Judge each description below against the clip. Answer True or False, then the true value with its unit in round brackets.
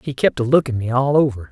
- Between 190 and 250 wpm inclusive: False (275 wpm)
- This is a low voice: True (130 Hz)